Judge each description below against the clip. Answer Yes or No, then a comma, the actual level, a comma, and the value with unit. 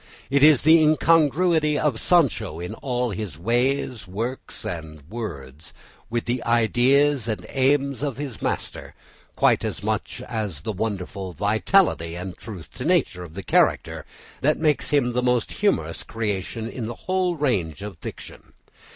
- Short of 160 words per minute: Yes, average, 150 wpm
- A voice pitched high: No, low, 120 Hz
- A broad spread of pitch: Yes, wide, 6.5 semitones